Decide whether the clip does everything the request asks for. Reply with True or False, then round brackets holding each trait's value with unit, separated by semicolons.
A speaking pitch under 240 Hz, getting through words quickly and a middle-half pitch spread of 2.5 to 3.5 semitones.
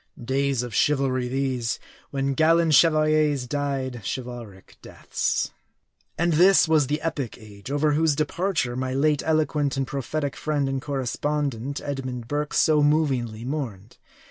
False (140 Hz; 135 wpm; 3.1 semitones)